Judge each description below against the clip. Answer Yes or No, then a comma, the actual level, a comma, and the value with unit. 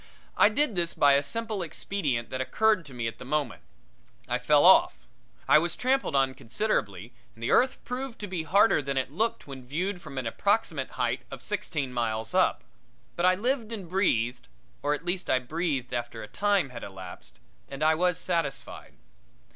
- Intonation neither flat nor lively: No, wide, 7.6 semitones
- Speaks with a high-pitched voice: No, medium, 150 Hz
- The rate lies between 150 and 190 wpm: Yes, average, 185 wpm